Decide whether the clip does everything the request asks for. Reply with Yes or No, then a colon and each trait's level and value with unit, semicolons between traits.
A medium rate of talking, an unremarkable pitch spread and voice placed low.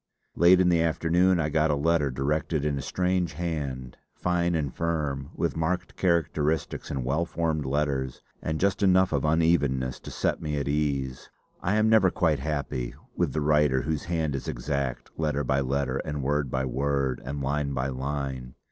Yes: average, 180 wpm; average, 3.5 semitones; very low, 75 Hz